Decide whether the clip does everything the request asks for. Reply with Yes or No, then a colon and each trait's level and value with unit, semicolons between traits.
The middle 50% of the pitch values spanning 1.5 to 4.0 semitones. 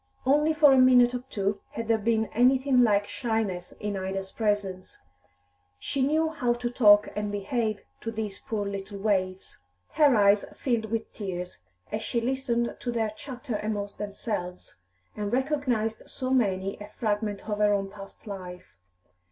Yes: average, 3.5 semitones